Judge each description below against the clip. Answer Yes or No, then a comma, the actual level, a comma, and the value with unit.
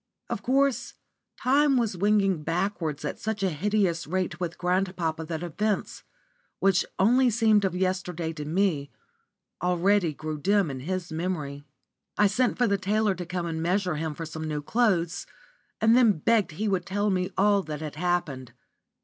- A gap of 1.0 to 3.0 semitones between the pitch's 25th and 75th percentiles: No, average, 4.2 semitones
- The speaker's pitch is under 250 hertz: Yes, medium, 185 Hz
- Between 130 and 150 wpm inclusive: No, average, 165 wpm